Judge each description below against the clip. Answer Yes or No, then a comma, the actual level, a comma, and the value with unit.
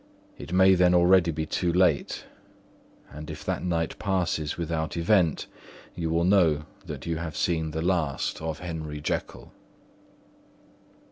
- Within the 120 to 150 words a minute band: Yes, average, 140 wpm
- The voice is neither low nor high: No, very low, 85 Hz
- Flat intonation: Yes, narrow, 2.2 semitones